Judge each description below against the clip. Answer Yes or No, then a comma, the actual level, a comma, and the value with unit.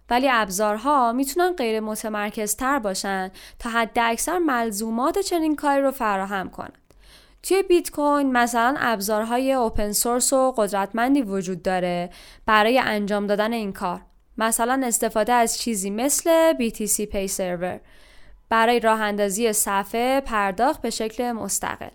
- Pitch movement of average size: Yes, average, 3.7 semitones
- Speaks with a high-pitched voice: Yes, high, 230 Hz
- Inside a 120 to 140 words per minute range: Yes, average, 130 wpm